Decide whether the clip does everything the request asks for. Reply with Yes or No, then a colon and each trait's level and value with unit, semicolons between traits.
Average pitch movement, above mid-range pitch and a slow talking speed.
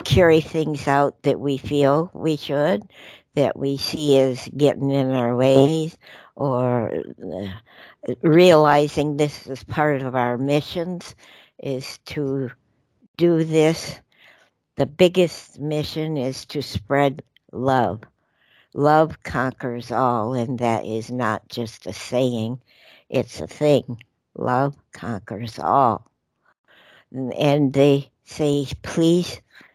No: average, 3.5 semitones; medium, 140 Hz; slow, 115 wpm